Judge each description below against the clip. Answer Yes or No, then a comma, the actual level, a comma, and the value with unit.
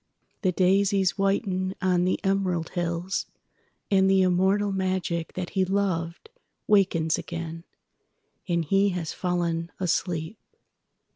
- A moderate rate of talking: No, slow, 95 wpm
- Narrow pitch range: Yes, narrow, 2.3 semitones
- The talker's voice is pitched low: No, medium, 185 Hz